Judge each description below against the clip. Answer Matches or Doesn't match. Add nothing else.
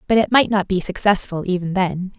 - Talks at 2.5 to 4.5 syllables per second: Doesn't match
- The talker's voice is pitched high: Matches